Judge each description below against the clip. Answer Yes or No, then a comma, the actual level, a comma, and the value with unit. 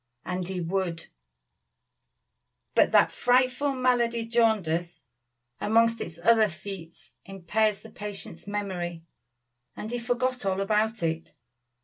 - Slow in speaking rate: Yes, slow, 110 wpm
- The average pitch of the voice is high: Yes, high, 205 Hz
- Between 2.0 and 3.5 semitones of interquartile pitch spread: No, average, 4.8 semitones